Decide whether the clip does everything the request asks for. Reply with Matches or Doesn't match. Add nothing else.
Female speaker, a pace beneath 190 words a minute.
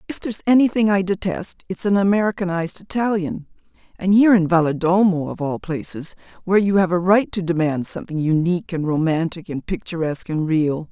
Matches